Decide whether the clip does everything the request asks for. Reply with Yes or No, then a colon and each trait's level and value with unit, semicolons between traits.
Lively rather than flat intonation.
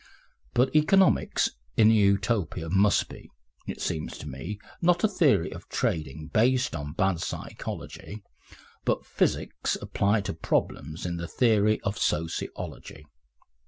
Yes: wide, 6.2 semitones